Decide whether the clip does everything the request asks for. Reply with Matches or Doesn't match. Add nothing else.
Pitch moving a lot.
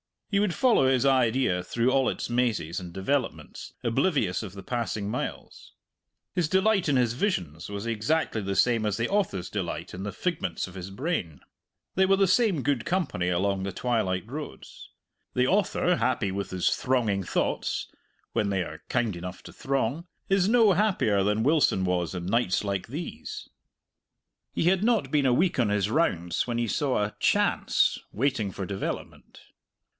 Matches